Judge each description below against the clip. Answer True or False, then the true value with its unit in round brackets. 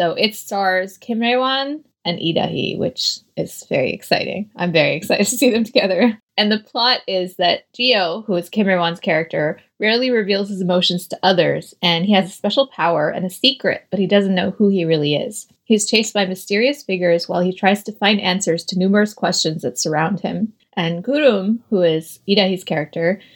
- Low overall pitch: False (195 Hz)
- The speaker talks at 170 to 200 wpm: True (195 wpm)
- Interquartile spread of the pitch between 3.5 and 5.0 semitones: True (3.8 semitones)